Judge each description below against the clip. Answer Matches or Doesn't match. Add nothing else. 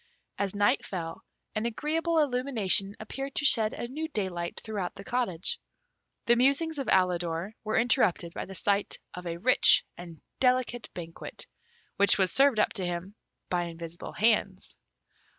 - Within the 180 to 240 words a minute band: Doesn't match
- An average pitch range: Doesn't match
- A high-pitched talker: Matches